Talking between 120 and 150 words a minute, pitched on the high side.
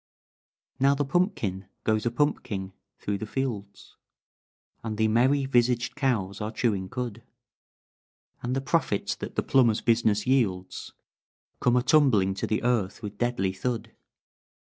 No: average, 140 wpm; low, 115 Hz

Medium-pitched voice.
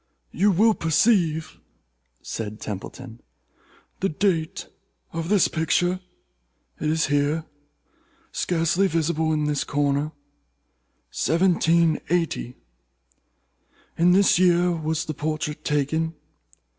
Yes: medium, 160 Hz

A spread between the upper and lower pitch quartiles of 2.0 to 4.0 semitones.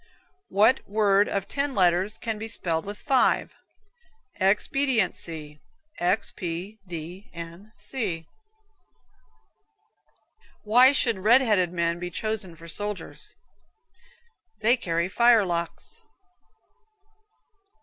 No: average, 4.4 semitones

